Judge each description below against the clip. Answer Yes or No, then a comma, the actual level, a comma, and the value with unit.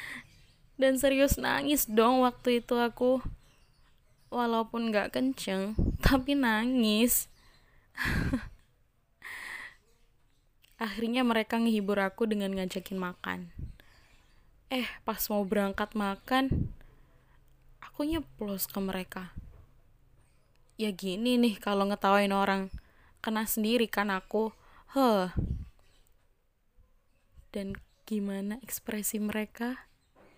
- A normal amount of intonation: Yes, average, 3.9 semitones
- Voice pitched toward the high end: Yes, high, 215 Hz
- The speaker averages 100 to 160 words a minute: No, slow, 85 wpm